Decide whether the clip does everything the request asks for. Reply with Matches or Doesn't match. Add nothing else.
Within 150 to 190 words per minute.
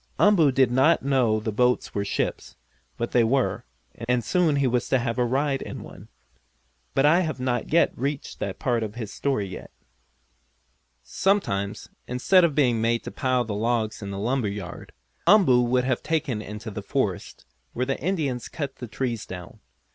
Matches